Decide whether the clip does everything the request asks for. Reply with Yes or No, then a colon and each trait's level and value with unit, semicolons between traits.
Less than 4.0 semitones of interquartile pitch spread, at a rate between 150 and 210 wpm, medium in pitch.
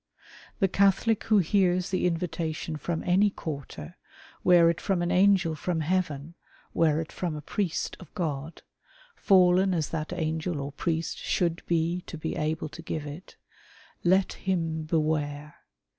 Yes: average, 2.8 semitones; average, 160 wpm; medium, 165 Hz